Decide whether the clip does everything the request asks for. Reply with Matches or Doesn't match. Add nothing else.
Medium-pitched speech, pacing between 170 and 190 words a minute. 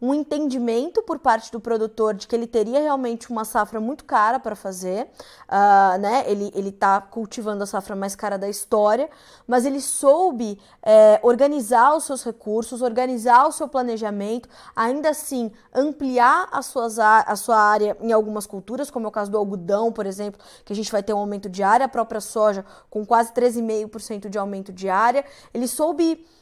Doesn't match